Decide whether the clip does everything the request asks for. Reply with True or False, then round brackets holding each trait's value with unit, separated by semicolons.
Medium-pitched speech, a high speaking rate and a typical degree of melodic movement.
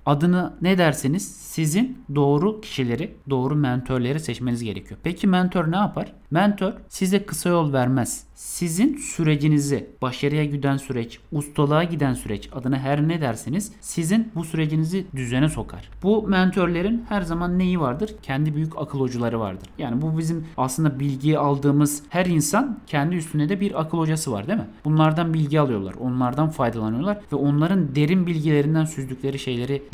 True (150 Hz; 150 wpm; 4.5 semitones)